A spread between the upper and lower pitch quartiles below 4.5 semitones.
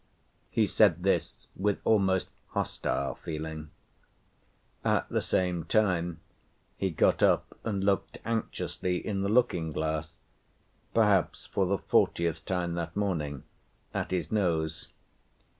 Yes: average, 3.6 semitones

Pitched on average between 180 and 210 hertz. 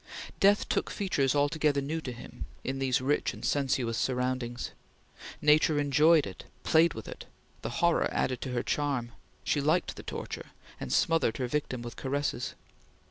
No: medium, 140 Hz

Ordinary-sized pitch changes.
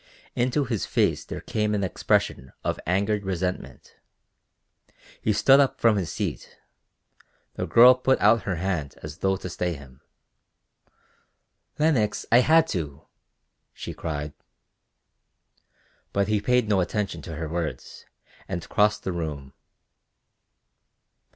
Yes: average, 5.0 semitones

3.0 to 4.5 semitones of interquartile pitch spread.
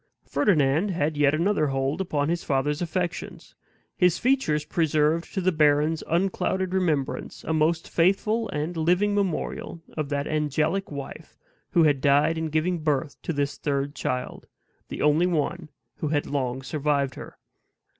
Yes: average, 3.4 semitones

